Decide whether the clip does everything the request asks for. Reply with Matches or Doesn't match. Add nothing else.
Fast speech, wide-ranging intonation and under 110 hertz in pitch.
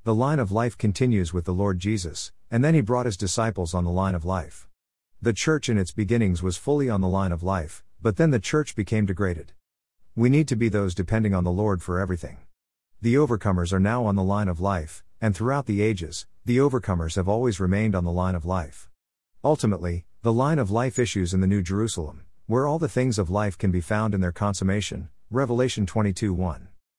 Doesn't match